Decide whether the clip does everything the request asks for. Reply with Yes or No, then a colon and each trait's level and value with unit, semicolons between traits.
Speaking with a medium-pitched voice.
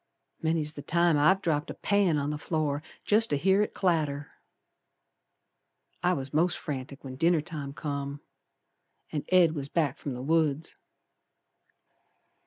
Yes: medium, 150 Hz